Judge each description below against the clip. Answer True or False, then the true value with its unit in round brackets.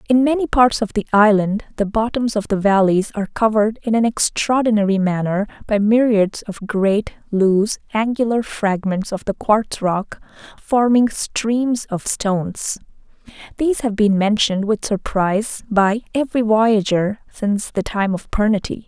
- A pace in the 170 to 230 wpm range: False (145 wpm)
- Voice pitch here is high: True (215 Hz)